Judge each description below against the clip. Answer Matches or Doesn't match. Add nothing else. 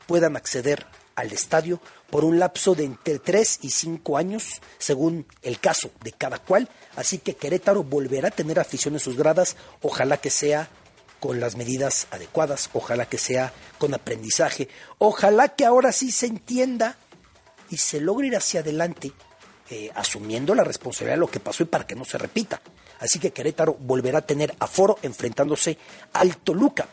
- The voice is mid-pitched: Matches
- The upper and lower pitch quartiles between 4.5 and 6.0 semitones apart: Matches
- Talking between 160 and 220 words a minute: Matches